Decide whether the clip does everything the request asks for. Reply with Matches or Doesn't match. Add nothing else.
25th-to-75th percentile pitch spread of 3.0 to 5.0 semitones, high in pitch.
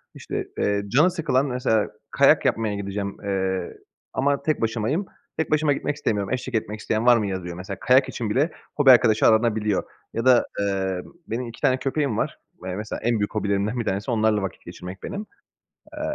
Doesn't match